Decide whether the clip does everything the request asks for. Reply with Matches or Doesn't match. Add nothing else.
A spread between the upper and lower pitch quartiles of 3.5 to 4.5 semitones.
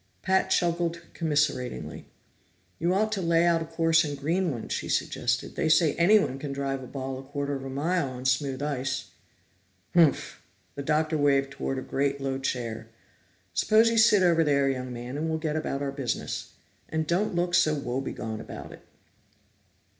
Matches